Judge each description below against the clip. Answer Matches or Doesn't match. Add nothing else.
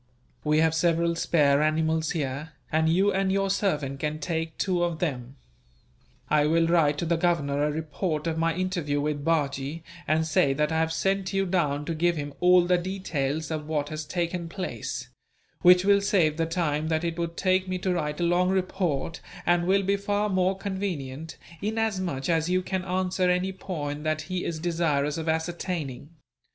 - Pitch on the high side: Doesn't match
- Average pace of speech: Matches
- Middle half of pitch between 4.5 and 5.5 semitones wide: Doesn't match